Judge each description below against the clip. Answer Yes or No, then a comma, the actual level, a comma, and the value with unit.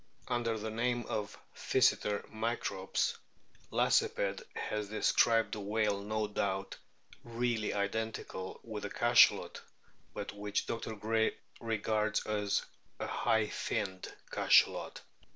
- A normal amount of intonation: No, narrow, 1.6 semitones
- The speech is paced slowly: Yes, slow, 115 wpm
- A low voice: Yes, low, 110 Hz